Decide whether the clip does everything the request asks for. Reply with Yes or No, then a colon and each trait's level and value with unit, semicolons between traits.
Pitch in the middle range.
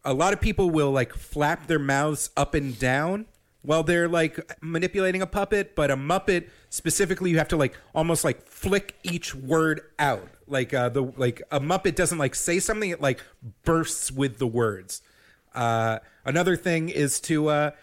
Yes: medium, 155 Hz